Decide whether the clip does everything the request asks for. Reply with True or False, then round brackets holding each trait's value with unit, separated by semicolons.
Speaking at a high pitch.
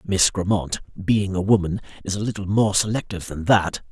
False (95 Hz)